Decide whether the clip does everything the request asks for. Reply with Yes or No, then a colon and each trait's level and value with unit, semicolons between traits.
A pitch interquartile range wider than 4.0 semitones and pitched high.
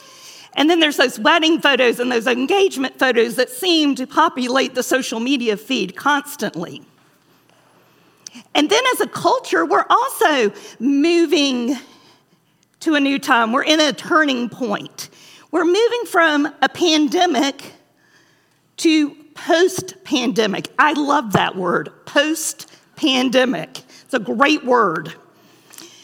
Yes: average, 4.5 semitones; very high, 290 Hz